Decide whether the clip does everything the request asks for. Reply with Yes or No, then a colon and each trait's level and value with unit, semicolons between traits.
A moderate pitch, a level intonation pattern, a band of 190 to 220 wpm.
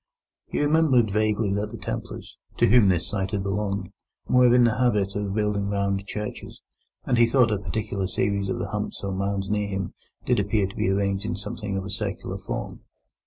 No: low, 100 Hz; narrow, 1.7 semitones; average, 200 wpm